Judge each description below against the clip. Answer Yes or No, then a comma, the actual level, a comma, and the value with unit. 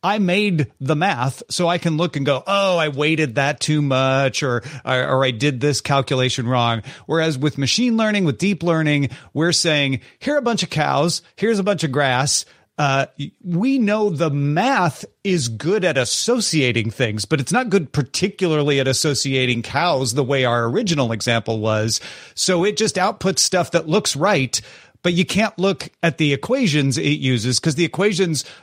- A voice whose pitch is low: No, medium, 150 Hz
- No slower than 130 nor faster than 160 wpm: No, average, 185 wpm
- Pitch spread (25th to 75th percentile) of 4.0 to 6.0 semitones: Yes, wide, 5.4 semitones